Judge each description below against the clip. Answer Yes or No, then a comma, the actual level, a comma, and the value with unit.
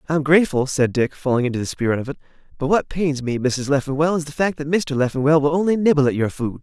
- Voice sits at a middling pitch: Yes, medium, 145 Hz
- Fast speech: Yes, fast, 255 wpm